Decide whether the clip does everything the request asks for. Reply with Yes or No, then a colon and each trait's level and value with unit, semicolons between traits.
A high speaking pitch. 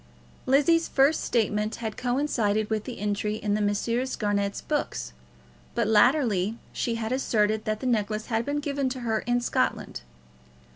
Yes: high, 225 Hz